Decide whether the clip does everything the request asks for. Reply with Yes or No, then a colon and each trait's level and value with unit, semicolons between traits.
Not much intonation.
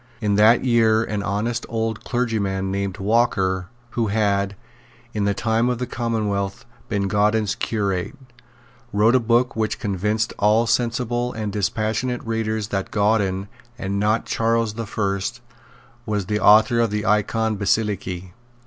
Yes: narrow, 2.3 semitones